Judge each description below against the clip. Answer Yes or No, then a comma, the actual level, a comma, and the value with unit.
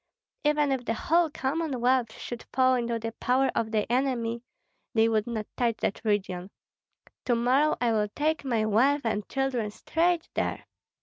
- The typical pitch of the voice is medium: No, high, 245 Hz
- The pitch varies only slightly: No, average, 3.3 semitones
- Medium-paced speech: Yes, average, 165 wpm